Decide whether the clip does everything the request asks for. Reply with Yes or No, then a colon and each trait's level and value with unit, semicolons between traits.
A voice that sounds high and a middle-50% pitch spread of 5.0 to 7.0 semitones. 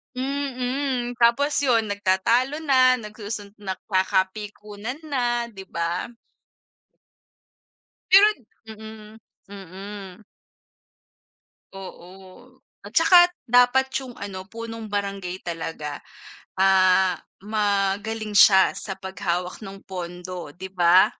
No: high, 205 Hz; average, 4.2 semitones